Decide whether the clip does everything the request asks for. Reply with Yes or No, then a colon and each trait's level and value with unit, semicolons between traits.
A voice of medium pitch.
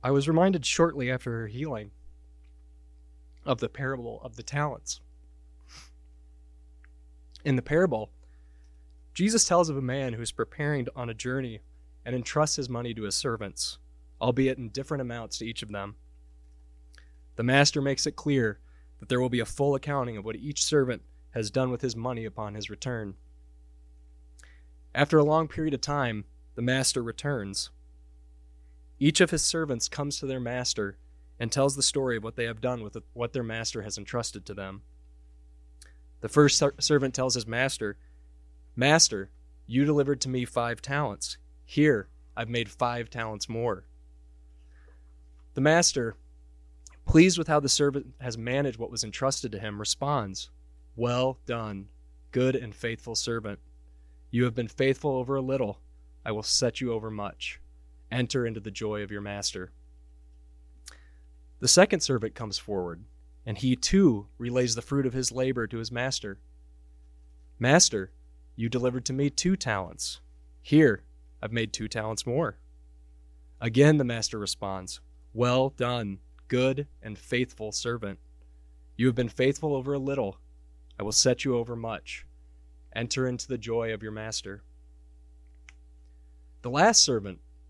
No: low, 110 Hz